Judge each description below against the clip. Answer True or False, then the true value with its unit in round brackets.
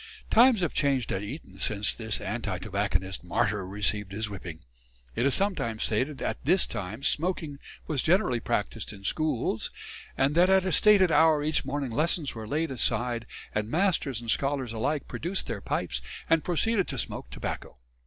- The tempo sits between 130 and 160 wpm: False (175 wpm)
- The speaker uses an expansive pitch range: True (7.3 semitones)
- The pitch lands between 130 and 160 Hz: True (135 Hz)